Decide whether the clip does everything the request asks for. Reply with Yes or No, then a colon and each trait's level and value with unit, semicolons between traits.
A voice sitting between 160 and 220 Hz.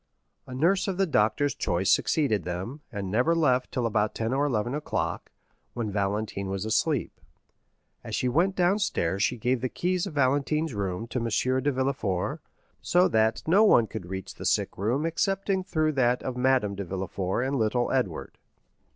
No: low, 125 Hz